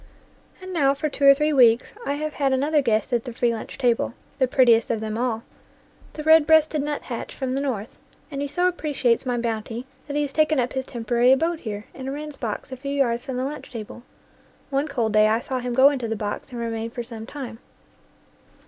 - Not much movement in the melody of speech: No, average, 3.6 semitones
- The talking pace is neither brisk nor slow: No, fast, 230 wpm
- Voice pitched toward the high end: Yes, very high, 260 Hz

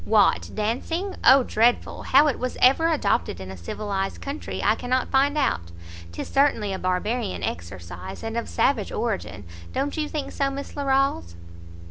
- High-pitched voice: Yes, high, 235 Hz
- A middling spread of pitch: No, wide, 6.6 semitones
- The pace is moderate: Yes, average, 160 wpm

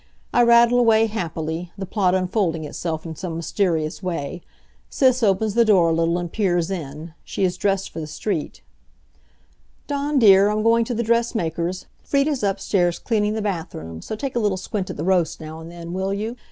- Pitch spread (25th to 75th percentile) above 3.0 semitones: Yes, average, 4.8 semitones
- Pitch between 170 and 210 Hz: Yes, high, 190 Hz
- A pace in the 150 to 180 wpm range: No, average, 190 wpm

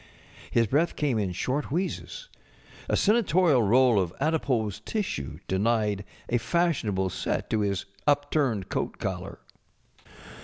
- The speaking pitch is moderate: No, low, 125 Hz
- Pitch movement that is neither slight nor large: No, wide, 7.0 semitones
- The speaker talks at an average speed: No, slow, 120 wpm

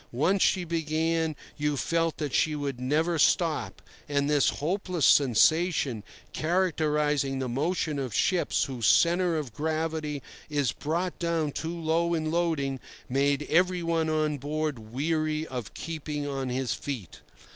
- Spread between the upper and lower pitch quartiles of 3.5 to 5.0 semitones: No, average, 2.9 semitones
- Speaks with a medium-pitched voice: Yes, medium, 155 Hz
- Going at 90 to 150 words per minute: Yes, slow, 135 wpm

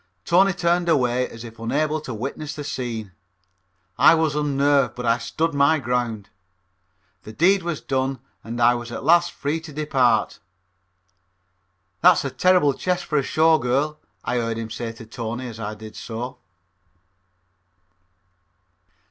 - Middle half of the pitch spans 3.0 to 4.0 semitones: No, average, 5.0 semitones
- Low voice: Yes, low, 130 Hz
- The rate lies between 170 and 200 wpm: No, average, 155 wpm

